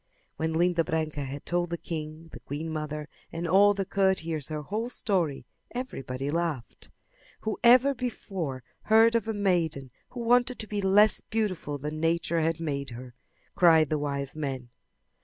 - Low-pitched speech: No, medium, 165 Hz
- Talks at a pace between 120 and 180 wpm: Yes, average, 160 wpm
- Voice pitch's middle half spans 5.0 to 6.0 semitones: Yes, wide, 5.4 semitones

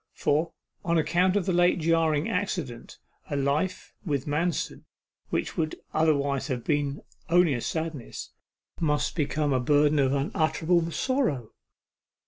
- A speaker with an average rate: No, slow, 130 wpm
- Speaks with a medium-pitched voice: Yes, medium, 155 Hz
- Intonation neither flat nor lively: Yes, average, 3.2 semitones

